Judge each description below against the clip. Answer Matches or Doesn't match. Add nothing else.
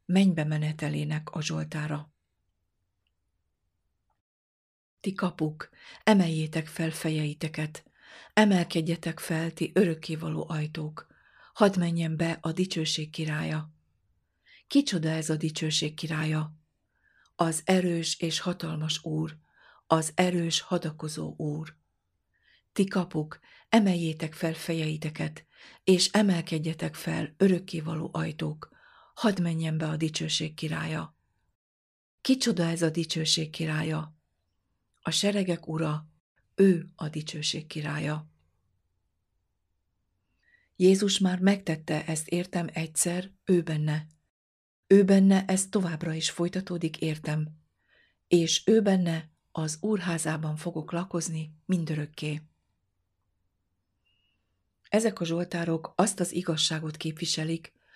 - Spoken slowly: Matches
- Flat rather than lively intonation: Matches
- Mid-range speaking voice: Matches